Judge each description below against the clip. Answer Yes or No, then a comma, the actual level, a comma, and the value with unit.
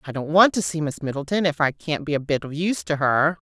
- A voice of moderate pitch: Yes, medium, 155 Hz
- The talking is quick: Yes, fast, 295 wpm